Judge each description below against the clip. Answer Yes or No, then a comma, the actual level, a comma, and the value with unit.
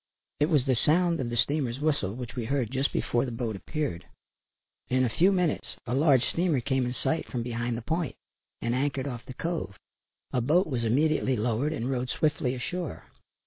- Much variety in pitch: No, average, 4.3 semitones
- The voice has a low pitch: Yes, low, 130 Hz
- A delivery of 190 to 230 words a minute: Yes, average, 195 wpm